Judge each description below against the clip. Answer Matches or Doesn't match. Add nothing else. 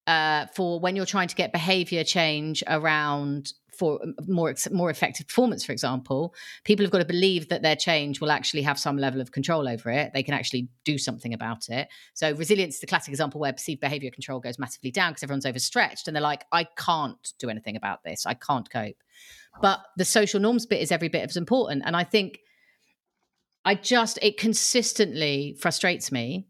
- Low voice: Doesn't match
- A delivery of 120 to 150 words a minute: Doesn't match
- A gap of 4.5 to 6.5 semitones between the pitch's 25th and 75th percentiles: Matches